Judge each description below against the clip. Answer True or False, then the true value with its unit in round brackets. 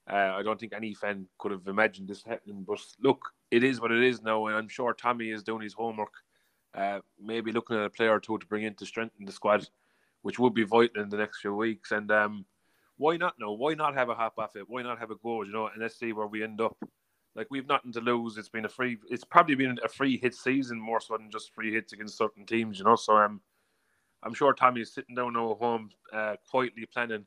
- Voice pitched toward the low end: True (110 Hz)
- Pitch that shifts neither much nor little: False (2.0 semitones)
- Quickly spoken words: True (260 wpm)